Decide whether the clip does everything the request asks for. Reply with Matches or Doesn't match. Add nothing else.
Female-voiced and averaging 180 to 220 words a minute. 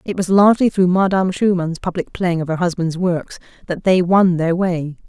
Matches